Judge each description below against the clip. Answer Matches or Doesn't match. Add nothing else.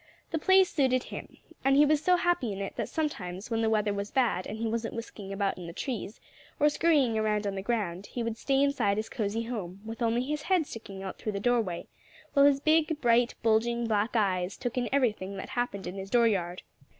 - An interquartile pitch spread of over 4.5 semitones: Matches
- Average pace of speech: Doesn't match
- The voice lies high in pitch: Matches